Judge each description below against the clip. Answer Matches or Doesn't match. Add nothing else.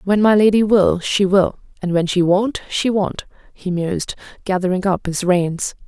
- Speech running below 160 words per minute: Doesn't match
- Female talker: Matches